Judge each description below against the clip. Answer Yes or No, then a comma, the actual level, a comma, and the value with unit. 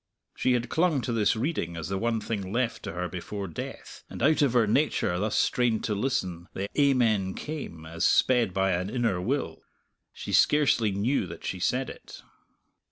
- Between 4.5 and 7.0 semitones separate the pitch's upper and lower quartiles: Yes, average, 5.3 semitones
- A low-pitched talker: Yes, low, 110 Hz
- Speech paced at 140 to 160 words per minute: No, average, 185 wpm